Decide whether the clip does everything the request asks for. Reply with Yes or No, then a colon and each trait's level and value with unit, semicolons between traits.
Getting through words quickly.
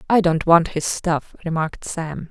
No: average, 180 wpm